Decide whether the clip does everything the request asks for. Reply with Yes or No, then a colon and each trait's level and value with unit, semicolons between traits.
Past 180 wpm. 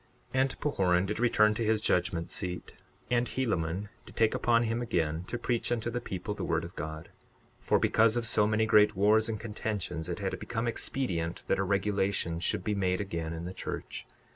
Yes: average, 195 wpm